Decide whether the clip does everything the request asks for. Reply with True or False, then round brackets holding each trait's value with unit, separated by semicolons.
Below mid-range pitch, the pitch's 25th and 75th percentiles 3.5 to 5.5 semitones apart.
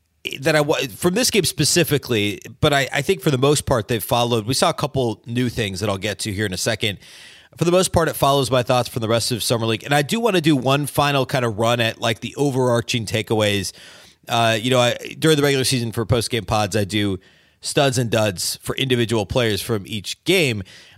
True (120 Hz; 4.2 semitones)